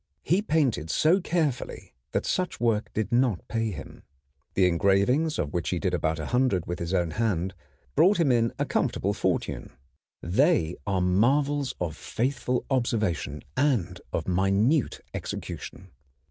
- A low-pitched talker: Yes, low, 110 Hz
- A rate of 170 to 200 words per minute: No, average, 145 wpm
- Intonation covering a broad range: Yes, wide, 7.0 semitones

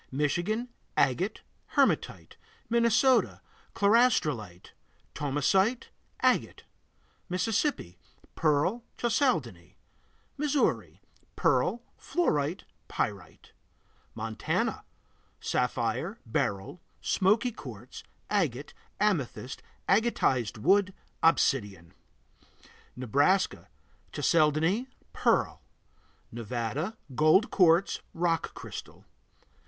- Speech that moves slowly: Yes, slow, 65 wpm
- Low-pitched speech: No, medium, 165 Hz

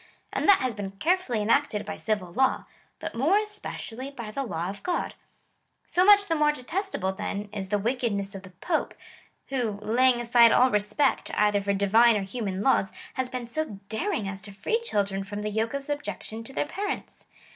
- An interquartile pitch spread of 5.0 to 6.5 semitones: Yes, wide, 5.6 semitones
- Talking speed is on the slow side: No, average, 195 wpm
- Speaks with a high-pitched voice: Yes, high, 230 Hz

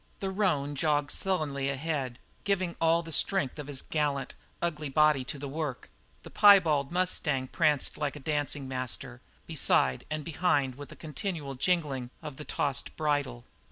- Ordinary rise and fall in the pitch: Yes, average, 3.1 semitones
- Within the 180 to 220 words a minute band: No, average, 155 wpm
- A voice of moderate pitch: Yes, medium, 150 Hz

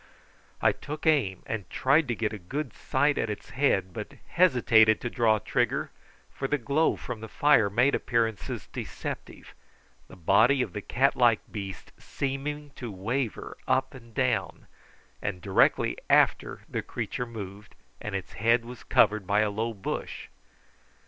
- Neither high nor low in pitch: No, low, 115 Hz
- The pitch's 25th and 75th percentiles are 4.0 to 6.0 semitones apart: Yes, average, 4.5 semitones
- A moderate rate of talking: Yes, average, 155 wpm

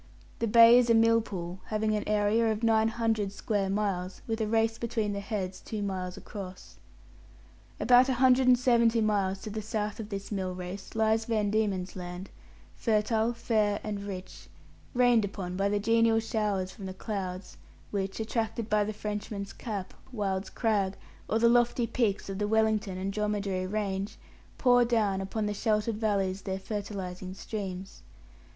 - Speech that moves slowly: No, average, 165 wpm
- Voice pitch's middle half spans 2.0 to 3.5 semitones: Yes, narrow, 2.4 semitones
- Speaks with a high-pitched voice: Yes, high, 210 Hz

